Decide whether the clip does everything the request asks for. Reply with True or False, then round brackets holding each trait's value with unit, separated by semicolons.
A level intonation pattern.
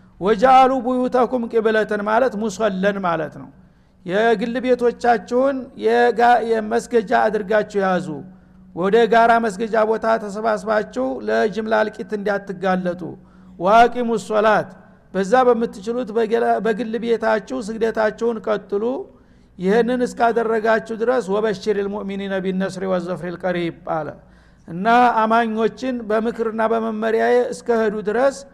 True (2.3 semitones)